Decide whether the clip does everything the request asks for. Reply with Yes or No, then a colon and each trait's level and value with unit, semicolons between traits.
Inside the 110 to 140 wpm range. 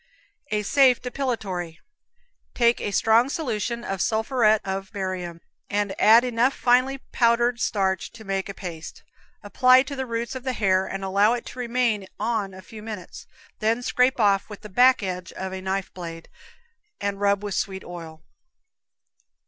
No: average, 165 wpm